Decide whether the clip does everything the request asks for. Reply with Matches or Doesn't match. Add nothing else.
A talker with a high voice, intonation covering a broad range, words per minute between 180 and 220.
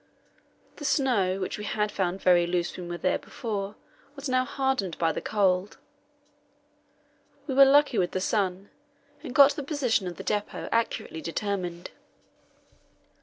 Doesn't match